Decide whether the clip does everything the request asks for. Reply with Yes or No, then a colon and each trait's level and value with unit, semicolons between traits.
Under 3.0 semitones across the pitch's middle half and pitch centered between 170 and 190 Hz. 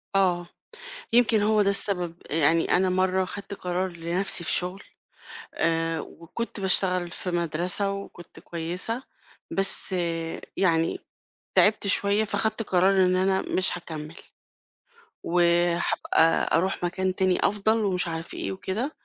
Yes: narrow, 2.5 semitones; medium, 185 Hz